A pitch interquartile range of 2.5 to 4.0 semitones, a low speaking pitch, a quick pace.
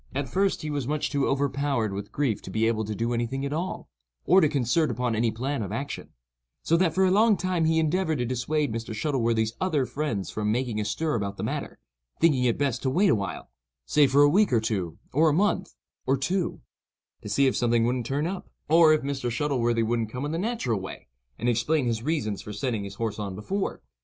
No: wide, 5.4 semitones; low, 130 Hz; fast, 220 wpm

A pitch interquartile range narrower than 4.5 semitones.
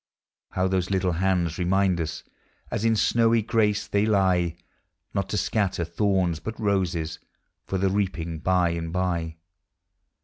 Yes: average, 3.0 semitones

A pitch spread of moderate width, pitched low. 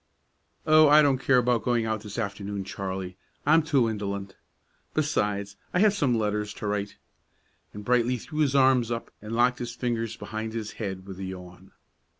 Yes: average, 3.9 semitones; low, 110 Hz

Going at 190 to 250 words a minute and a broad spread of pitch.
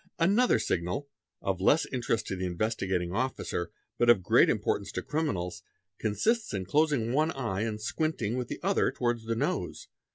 No: average, 170 wpm; wide, 7.2 semitones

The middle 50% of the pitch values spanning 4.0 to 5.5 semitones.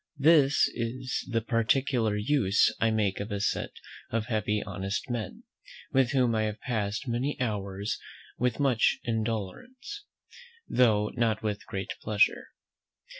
No: average, 3.5 semitones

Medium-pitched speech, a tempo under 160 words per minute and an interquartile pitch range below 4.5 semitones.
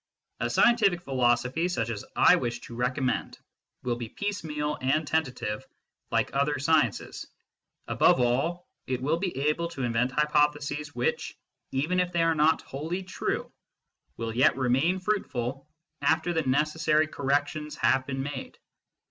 Yes: medium, 145 Hz; average, 140 wpm; average, 4.1 semitones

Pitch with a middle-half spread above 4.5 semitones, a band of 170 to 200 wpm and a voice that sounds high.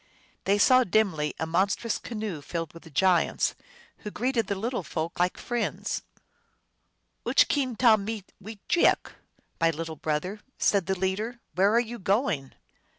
No: average, 5.3 semitones; average, 160 wpm; high, 195 Hz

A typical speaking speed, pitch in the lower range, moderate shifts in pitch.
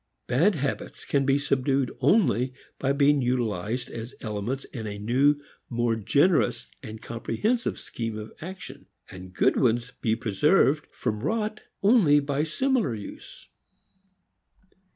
No: slow, 130 wpm; low, 130 Hz; average, 4.5 semitones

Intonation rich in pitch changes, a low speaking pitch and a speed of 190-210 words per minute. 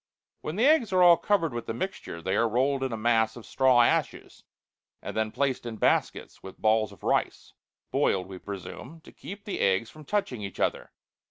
Yes: wide, 7.1 semitones; low, 120 Hz; average, 200 wpm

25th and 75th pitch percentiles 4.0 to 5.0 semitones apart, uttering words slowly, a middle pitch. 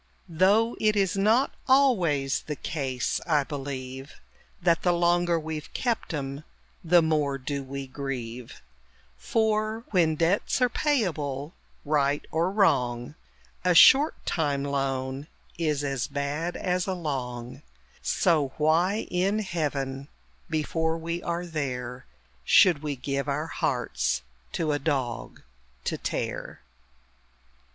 Yes: average, 4.5 semitones; slow, 120 wpm; medium, 155 Hz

